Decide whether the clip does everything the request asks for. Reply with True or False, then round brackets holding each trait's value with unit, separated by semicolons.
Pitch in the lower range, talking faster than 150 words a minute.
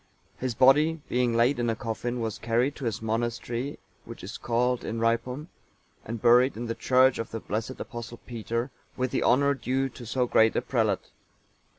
True (120 Hz; 185 wpm)